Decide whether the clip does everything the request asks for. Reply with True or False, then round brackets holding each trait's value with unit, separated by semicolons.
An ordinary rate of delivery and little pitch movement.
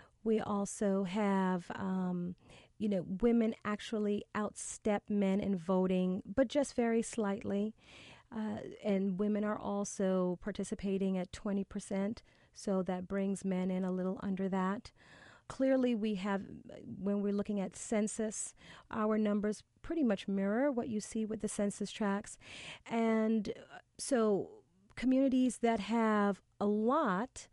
False (130 wpm; 2.2 semitones)